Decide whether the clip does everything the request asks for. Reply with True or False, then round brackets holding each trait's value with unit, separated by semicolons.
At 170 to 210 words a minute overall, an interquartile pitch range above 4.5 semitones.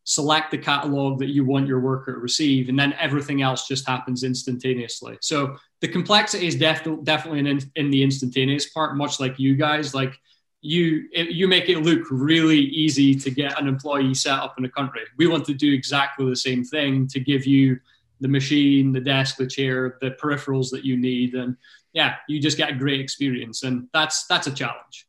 False (205 wpm; 2.4 semitones)